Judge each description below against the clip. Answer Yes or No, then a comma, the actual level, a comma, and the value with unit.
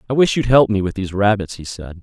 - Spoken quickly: Yes, fast, 295 wpm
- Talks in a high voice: No, low, 105 Hz